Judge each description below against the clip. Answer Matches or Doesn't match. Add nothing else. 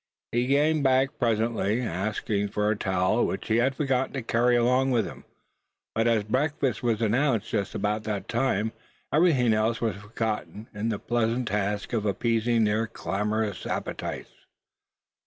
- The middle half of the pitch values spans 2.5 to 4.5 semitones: Matches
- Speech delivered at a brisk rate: Doesn't match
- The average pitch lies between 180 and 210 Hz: Doesn't match